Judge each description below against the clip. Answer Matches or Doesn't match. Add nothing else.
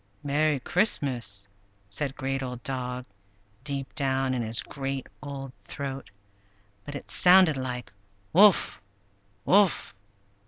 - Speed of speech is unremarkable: Doesn't match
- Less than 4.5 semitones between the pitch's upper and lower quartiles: Matches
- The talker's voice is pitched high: Doesn't match